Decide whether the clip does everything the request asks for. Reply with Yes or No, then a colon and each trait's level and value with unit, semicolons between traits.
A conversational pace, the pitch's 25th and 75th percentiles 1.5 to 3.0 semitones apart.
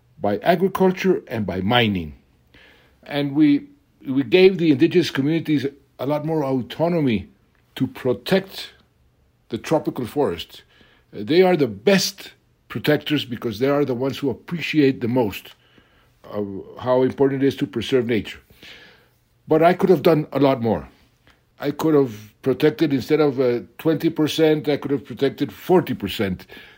No: average, 150 wpm; average, 4.5 semitones